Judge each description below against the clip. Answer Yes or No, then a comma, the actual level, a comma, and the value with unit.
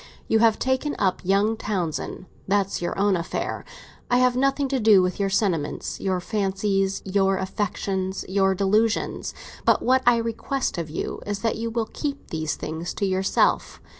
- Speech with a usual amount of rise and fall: Yes, average, 3.2 semitones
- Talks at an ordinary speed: Yes, average, 165 wpm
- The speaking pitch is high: Yes, high, 200 Hz